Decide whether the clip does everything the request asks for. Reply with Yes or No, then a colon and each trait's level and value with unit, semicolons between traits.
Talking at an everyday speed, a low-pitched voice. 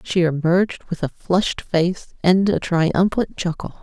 No: average, 155 wpm; medium, 170 Hz